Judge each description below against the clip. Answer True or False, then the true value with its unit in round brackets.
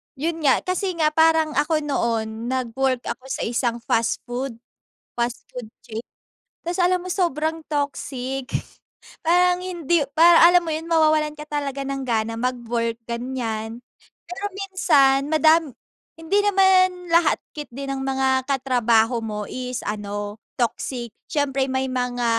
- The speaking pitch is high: True (270 Hz)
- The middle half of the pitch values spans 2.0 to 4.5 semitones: False (5.2 semitones)